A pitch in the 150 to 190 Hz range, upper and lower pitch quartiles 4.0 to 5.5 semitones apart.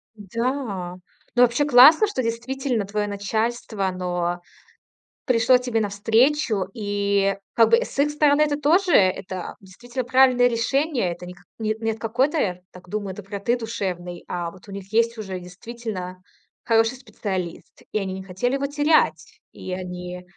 No: high, 220 Hz; average, 4.9 semitones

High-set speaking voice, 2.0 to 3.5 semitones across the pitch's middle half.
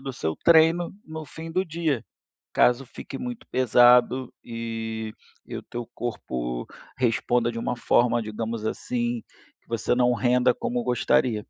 No: low, 120 Hz; narrow, 2.5 semitones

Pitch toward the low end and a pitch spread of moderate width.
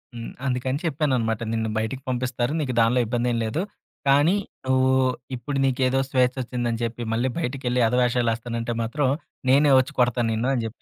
No: low, 125 Hz; narrow, 2.0 semitones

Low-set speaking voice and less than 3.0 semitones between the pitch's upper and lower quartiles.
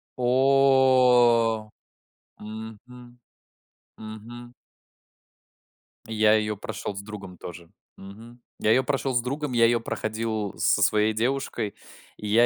Yes: low, 115 Hz; narrow, 2.6 semitones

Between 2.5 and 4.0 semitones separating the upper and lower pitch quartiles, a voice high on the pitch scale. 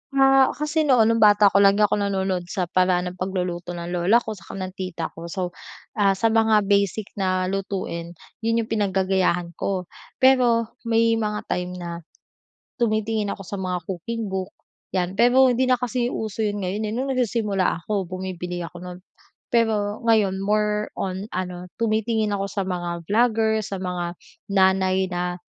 Yes: average, 3.3 semitones; high, 200 Hz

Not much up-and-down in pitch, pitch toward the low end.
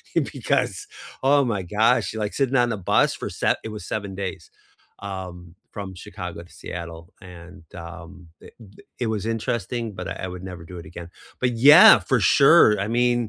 No: average, 4.3 semitones; low, 100 Hz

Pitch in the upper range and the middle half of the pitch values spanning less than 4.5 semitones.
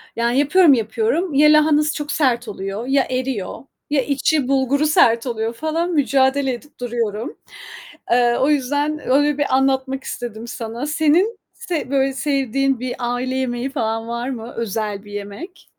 Yes: very high, 265 Hz; average, 3.7 semitones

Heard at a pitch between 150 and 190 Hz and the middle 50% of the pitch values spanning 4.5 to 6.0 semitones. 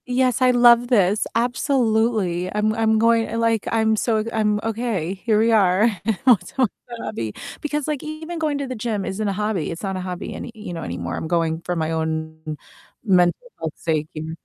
No: high, 215 Hz; average, 5.2 semitones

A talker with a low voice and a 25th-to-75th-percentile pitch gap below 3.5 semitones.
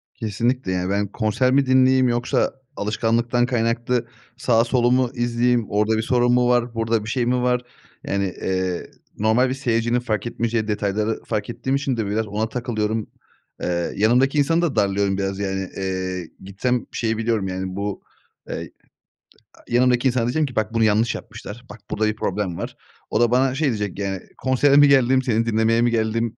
Yes: low, 115 Hz; average, 2.9 semitones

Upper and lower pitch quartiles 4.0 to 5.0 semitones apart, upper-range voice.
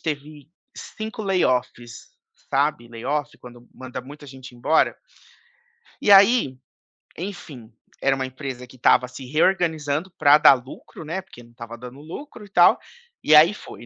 No: average, 4.4 semitones; medium, 140 Hz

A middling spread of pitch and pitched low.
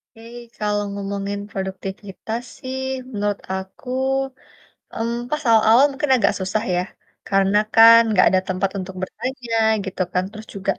No: average, 3.2 semitones; high, 205 Hz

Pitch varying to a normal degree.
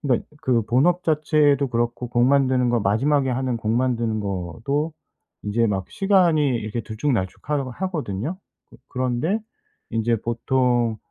Yes: average, 4.1 semitones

